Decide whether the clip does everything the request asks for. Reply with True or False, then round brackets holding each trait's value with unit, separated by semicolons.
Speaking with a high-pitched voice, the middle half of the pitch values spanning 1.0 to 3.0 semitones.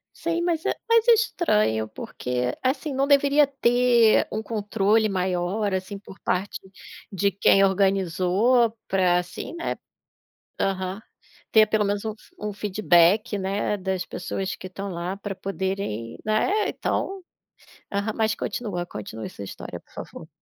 False (200 Hz; 3.5 semitones)